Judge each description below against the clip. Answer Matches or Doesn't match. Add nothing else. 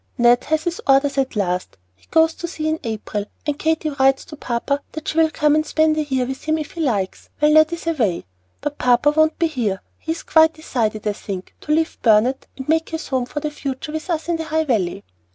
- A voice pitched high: Matches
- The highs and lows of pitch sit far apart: Doesn't match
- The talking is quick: Matches